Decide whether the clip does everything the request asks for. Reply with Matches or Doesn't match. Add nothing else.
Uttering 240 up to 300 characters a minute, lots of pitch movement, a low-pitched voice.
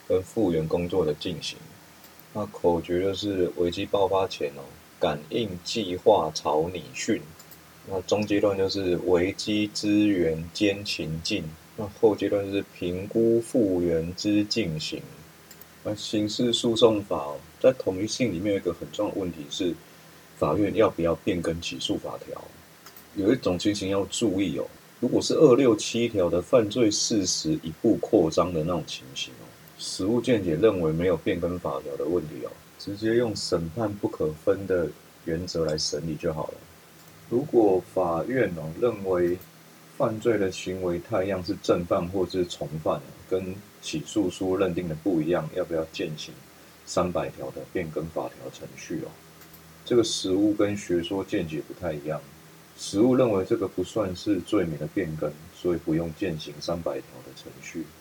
Doesn't match